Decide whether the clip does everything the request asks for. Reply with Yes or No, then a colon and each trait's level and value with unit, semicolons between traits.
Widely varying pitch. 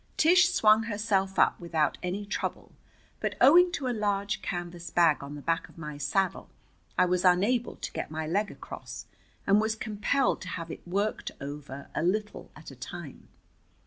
No: average, 4.5 semitones